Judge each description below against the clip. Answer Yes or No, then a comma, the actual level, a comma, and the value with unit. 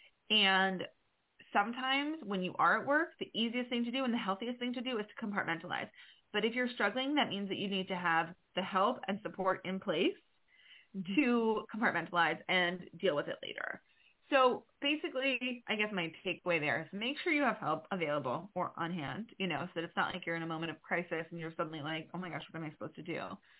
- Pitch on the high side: Yes, high, 195 Hz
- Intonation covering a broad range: Yes, wide, 6.4 semitones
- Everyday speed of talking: No, fast, 225 wpm